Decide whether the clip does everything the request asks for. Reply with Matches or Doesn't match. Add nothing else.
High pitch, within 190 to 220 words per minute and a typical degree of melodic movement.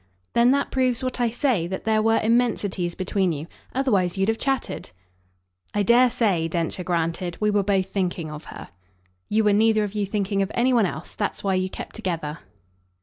Matches